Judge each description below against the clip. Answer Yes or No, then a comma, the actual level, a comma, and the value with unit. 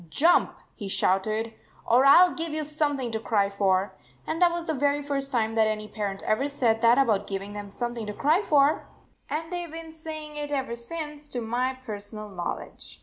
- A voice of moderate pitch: No, very high, 255 Hz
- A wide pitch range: Yes, wide, 5.8 semitones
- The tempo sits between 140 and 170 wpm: No, fast, 205 wpm